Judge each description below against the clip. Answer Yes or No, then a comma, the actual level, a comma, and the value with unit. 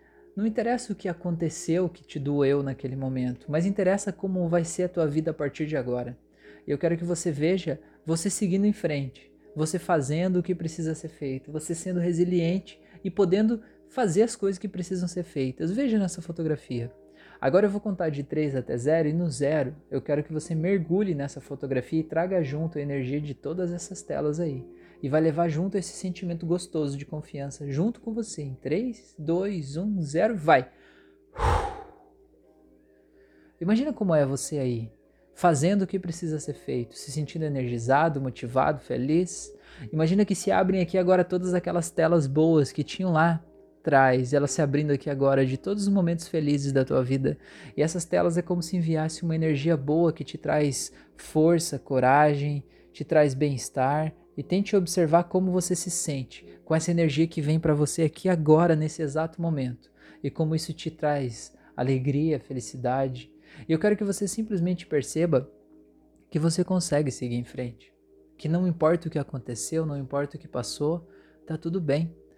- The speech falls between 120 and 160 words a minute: No, average, 175 wpm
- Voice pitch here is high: No, medium, 155 Hz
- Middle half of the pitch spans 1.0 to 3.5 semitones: No, average, 4.1 semitones